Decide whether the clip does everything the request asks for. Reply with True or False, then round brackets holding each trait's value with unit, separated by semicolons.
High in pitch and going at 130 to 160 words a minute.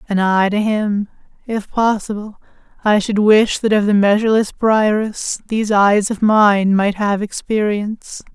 True (210 Hz; 150 wpm)